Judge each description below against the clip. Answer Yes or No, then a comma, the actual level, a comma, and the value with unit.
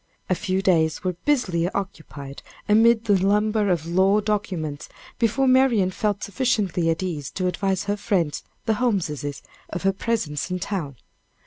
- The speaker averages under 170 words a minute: Yes, average, 150 wpm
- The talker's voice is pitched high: Yes, high, 195 Hz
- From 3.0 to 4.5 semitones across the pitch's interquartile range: Yes, average, 3.9 semitones